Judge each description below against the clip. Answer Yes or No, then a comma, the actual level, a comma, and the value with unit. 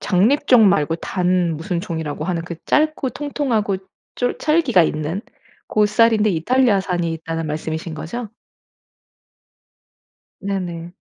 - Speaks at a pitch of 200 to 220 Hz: No, medium, 185 Hz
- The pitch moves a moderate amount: No, wide, 5.8 semitones